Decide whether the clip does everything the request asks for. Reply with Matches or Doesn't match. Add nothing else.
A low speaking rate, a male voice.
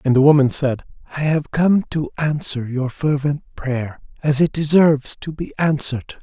Doesn't match